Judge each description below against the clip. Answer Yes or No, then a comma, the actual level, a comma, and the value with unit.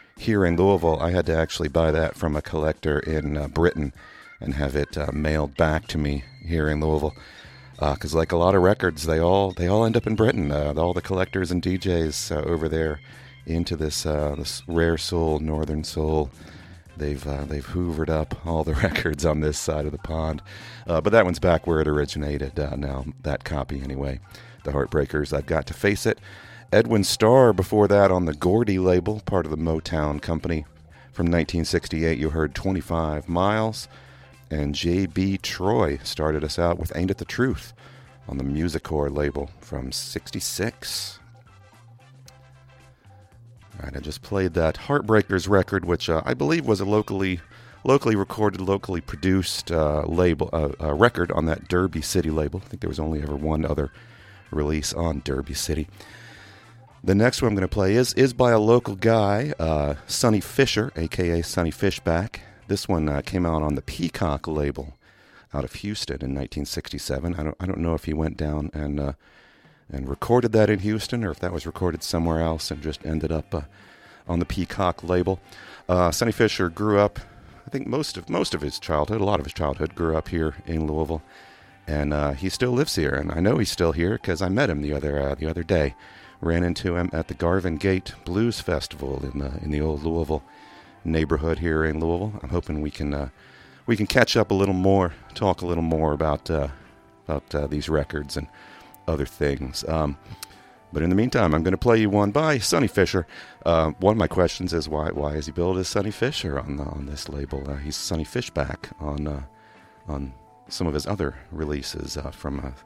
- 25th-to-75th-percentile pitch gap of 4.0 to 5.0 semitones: Yes, average, 4.6 semitones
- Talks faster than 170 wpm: Yes, average, 200 wpm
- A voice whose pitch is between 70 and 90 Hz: Yes, very low, 85 Hz